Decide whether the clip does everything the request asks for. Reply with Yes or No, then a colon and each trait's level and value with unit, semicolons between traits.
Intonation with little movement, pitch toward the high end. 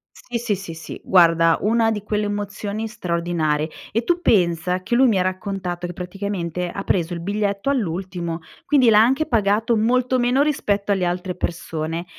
No: average, 4.2 semitones; high, 195 Hz